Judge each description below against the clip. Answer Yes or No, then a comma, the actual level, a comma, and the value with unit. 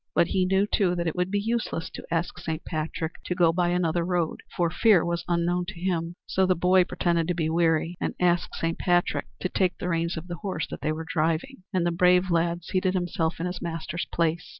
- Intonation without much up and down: Yes, narrow, 1.5 semitones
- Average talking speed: No, fast, 230 wpm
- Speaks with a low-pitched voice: No, medium, 175 Hz